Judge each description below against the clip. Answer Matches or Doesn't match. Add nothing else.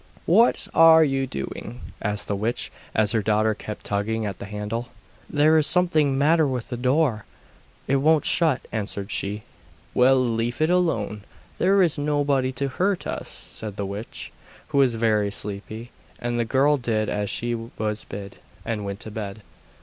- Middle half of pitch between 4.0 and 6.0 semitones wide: Matches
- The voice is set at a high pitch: Doesn't match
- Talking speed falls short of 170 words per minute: Doesn't match